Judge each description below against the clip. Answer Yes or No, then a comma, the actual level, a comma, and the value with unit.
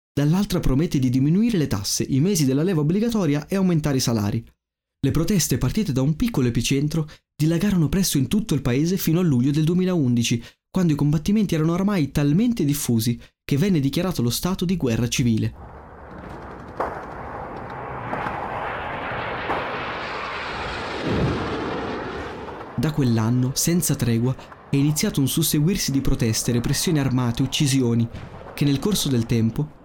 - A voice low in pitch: No, medium, 145 Hz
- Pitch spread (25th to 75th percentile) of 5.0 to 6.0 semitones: Yes, average, 5.3 semitones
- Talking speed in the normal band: Yes, average, 135 wpm